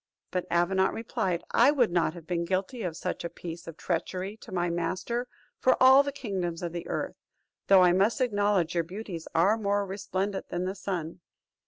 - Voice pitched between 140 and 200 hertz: Yes, medium, 185 Hz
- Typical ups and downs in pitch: Yes, average, 3.1 semitones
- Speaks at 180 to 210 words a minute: Yes, average, 190 wpm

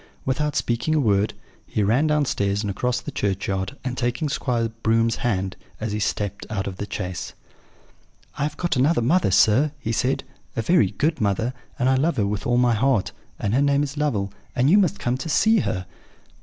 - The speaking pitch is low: Yes, low, 120 Hz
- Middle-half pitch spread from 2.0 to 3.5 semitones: No, wide, 5.6 semitones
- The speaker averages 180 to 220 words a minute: Yes, average, 200 wpm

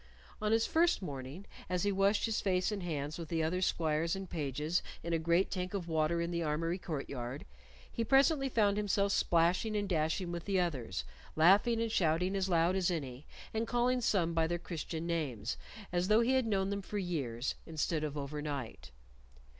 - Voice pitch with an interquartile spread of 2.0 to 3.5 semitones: No, average, 4.3 semitones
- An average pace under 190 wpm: No, average, 195 wpm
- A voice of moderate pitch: Yes, medium, 175 Hz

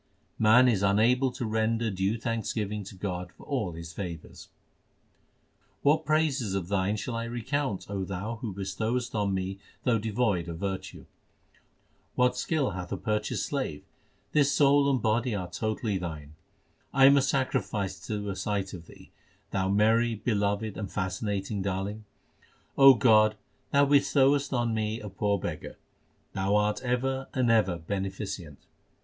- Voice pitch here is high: No, low, 105 Hz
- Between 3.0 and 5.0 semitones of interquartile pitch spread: Yes, average, 4.3 semitones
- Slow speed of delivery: No, average, 150 wpm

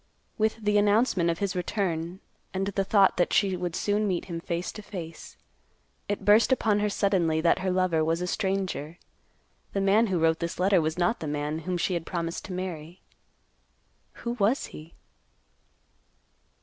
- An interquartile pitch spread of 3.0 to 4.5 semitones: Yes, average, 3.3 semitones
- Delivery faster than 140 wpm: Yes, average, 175 wpm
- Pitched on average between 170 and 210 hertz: Yes, medium, 185 Hz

